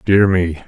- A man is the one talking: Yes, male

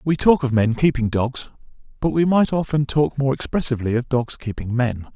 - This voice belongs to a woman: No, male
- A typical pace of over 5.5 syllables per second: No, 5.3 syllables/s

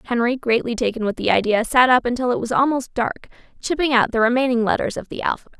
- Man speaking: No, female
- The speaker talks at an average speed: No, fast, 225 wpm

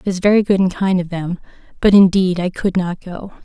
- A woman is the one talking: Yes, female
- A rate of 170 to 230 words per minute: No, fast, 245 wpm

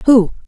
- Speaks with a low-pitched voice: No, high, 225 Hz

